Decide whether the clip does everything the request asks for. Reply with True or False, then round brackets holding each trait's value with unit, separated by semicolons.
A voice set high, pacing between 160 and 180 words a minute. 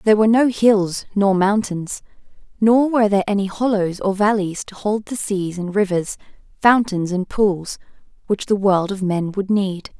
True (200 Hz; 175 wpm)